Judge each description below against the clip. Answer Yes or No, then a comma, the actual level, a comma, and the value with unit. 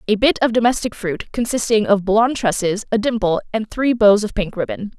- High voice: Yes, high, 215 Hz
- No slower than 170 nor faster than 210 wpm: Yes, fast, 205 wpm